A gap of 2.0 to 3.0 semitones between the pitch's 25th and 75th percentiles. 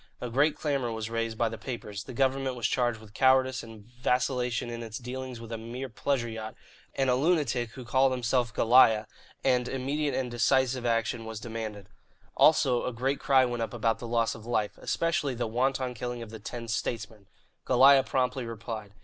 Yes: narrow, 2.5 semitones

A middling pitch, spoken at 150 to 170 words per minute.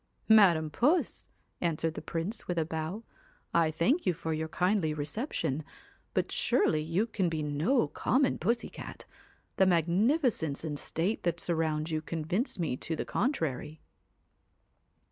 Yes: medium, 165 Hz; average, 160 wpm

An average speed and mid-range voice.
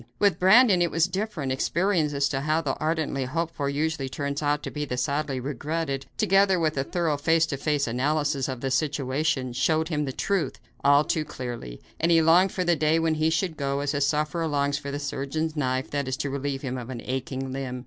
No: fast, 220 wpm; medium, 145 Hz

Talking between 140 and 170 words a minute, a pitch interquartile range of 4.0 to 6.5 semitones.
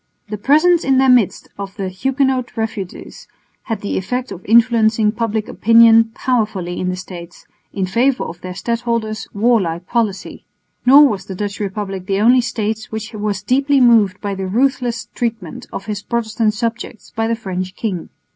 No: average, 165 wpm; average, 3.5 semitones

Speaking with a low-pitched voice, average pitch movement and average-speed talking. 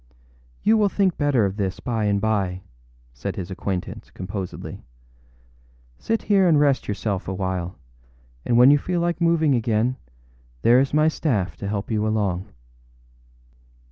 No: low, 110 Hz; wide, 7.2 semitones; average, 155 wpm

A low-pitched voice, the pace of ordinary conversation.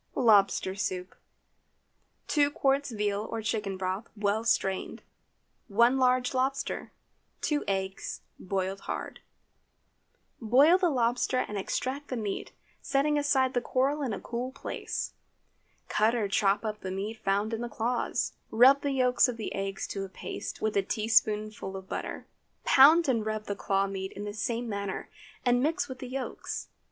No: high, 225 Hz; average, 155 wpm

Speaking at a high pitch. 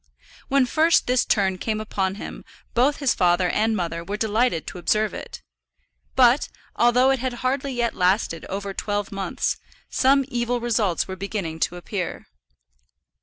Yes: high, 215 Hz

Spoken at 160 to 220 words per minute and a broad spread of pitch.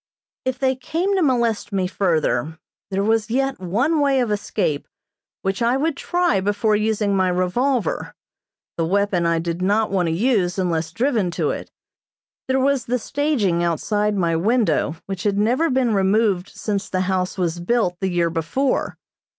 Yes: average, 165 wpm; wide, 5.7 semitones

